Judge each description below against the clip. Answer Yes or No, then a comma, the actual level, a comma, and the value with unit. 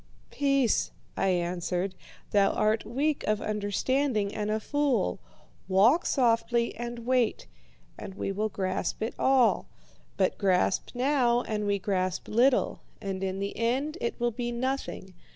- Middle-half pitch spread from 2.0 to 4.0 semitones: No, average, 4.4 semitones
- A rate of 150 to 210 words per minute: No, average, 140 wpm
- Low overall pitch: No, high, 220 Hz